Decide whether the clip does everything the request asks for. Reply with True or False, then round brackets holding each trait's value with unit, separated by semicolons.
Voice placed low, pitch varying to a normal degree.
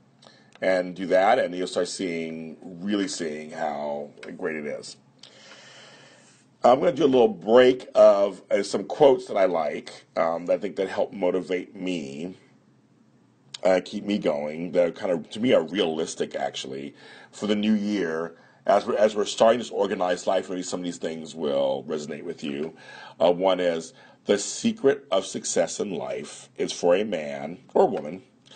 True (90 Hz; 4.0 semitones)